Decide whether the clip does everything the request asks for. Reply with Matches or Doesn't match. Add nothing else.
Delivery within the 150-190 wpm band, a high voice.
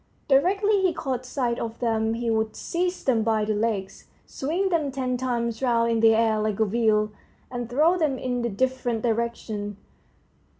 Matches